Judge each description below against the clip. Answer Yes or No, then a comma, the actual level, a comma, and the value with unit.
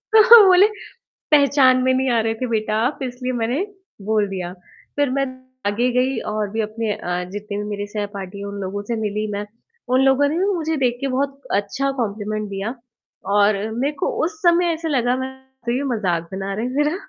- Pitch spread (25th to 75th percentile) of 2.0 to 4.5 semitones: No, average, 5.0 semitones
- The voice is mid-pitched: No, high, 235 Hz